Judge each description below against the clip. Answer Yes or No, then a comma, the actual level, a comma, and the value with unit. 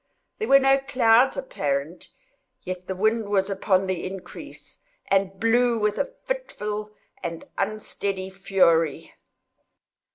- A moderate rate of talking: No, slow, 120 wpm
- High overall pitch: Yes, high, 200 Hz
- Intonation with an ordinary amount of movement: Yes, average, 3.5 semitones